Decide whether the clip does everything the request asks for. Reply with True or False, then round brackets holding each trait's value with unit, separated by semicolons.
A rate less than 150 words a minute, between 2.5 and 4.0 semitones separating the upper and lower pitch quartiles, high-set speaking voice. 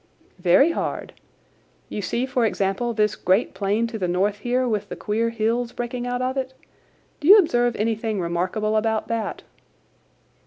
False (160 wpm; 2.9 semitones; 225 Hz)